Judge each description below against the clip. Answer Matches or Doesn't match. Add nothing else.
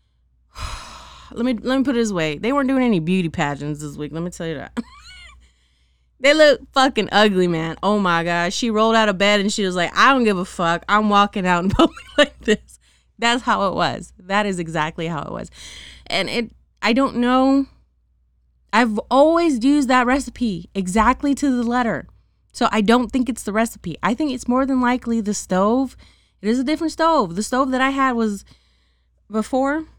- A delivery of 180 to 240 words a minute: Matches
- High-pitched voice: Matches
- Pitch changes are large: Matches